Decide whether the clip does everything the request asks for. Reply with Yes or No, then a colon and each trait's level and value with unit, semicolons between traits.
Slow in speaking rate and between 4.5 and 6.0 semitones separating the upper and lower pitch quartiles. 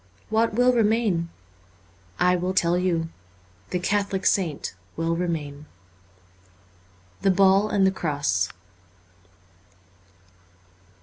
Yes: slow, 100 wpm; average, 5.2 semitones